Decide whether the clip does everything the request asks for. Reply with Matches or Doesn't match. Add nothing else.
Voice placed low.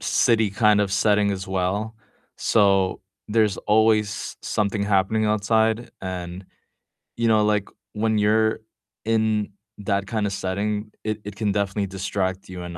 Matches